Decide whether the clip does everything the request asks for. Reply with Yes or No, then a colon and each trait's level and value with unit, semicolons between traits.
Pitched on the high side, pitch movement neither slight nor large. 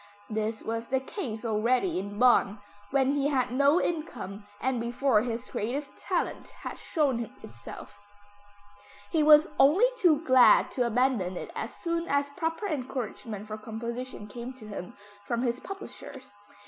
Yes: very high, 255 Hz; average, 4.4 semitones